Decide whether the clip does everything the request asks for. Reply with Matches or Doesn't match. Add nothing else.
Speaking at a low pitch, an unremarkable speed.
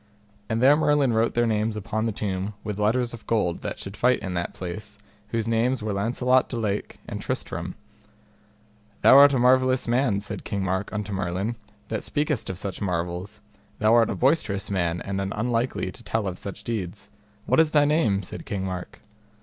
Matches